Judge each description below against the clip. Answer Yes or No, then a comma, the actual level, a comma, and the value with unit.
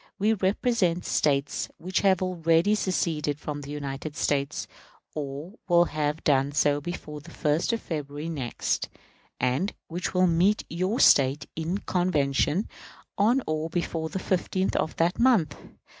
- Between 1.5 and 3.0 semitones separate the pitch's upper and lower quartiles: No, average, 4.1 semitones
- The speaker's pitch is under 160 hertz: No, medium, 165 Hz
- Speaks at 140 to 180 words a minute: Yes, average, 145 wpm